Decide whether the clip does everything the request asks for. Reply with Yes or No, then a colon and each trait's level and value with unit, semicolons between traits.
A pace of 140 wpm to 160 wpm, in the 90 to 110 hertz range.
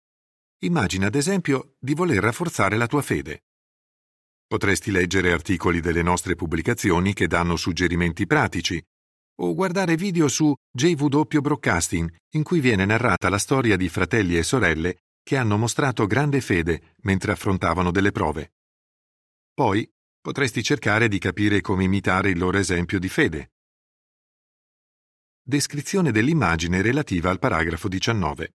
No: average, 130 wpm; low, 100 Hz